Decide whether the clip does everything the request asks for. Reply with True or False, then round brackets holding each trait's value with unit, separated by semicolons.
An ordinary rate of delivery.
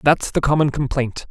True (185 wpm)